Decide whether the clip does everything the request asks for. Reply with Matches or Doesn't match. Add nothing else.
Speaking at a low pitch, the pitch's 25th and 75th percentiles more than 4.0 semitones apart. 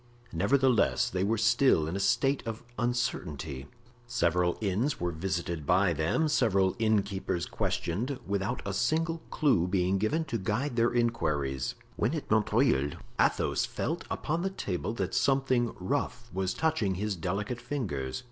Matches